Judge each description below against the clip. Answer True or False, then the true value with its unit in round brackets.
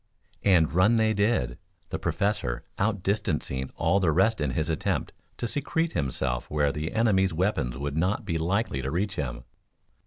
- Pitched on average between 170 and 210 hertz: False (85 Hz)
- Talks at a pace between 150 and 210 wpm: True (160 wpm)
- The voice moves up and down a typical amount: False (5.7 semitones)